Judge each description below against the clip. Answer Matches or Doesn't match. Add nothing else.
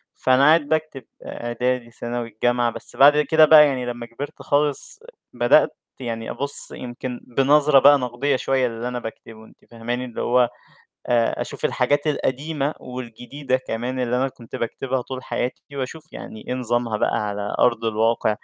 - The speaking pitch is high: Doesn't match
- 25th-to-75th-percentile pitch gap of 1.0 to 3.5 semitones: Matches